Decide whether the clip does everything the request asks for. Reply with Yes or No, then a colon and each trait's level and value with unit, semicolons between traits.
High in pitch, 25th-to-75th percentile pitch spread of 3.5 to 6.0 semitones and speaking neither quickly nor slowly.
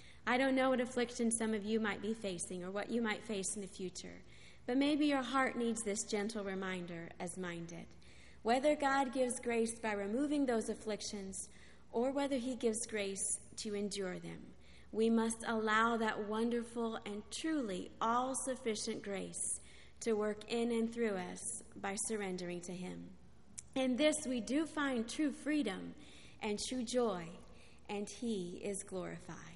Yes: high, 220 Hz; average, 3.9 semitones; average, 160 wpm